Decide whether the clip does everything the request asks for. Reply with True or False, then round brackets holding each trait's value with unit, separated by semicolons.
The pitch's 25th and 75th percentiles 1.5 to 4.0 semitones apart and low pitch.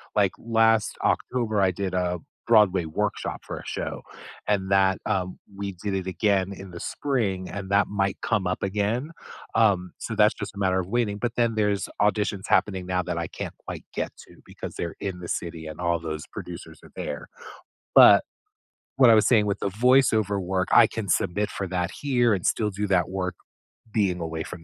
True (2.7 semitones; 100 Hz)